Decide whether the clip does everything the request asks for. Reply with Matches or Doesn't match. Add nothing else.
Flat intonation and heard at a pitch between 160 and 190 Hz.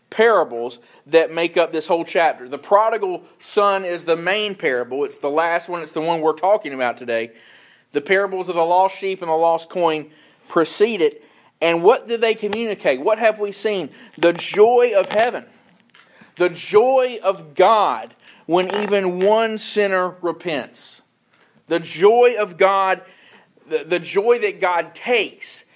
Doesn't match